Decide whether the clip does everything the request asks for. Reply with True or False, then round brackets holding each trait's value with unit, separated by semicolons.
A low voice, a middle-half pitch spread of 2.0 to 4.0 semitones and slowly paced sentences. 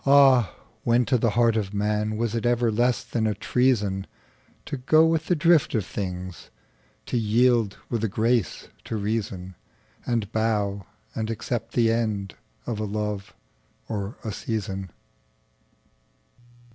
True (110 Hz; 2.9 semitones; 125 wpm)